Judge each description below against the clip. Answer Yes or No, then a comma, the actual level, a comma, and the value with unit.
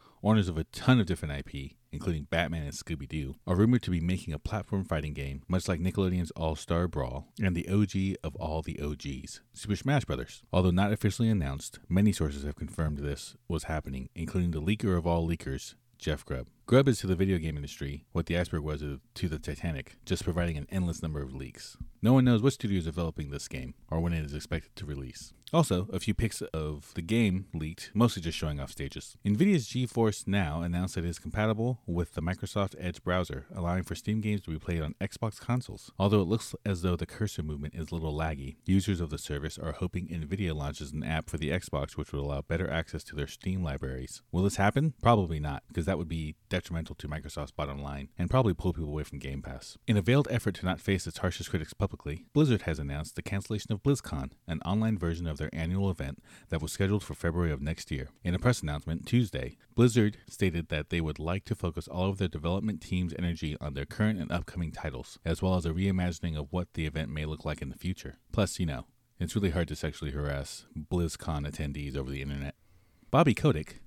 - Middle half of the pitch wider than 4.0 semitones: Yes, average, 4.4 semitones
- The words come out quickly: Yes, fast, 220 wpm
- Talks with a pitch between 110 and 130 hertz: No, very low, 85 Hz